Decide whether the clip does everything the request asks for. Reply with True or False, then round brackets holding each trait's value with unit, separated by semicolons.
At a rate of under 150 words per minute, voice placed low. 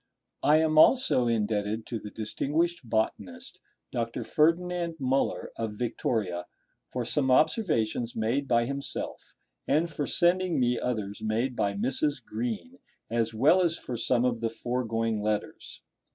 True (140 wpm; 120 Hz)